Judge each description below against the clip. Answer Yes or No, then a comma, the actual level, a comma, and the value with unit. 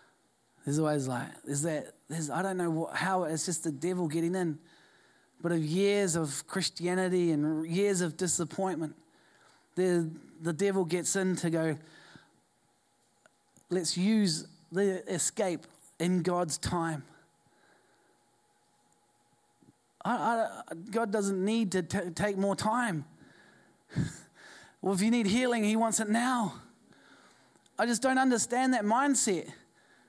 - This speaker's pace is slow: Yes, slow, 130 wpm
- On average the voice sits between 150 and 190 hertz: Yes, medium, 185 Hz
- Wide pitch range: No, average, 4.4 semitones